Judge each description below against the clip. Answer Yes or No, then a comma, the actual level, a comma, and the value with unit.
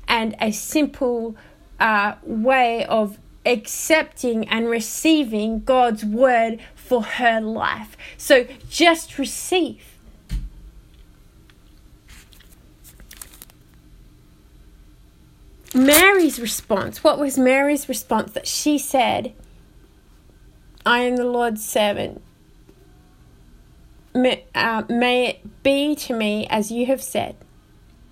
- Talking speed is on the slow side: Yes, slow, 90 wpm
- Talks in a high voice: Yes, high, 240 Hz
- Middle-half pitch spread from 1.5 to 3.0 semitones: No, average, 3.8 semitones